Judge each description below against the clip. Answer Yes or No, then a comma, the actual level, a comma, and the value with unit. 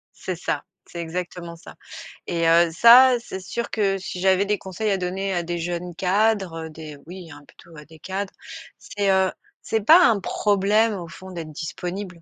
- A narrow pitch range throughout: No, average, 3.0 semitones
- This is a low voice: No, medium, 185 Hz